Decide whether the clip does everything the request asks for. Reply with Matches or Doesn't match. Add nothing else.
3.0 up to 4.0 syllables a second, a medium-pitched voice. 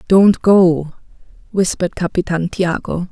Matches